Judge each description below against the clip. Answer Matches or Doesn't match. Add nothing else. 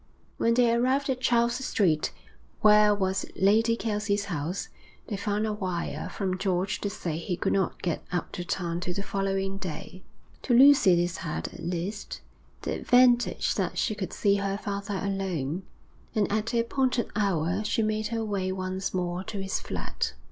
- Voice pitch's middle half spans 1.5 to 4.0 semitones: Matches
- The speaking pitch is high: Matches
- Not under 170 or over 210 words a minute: Matches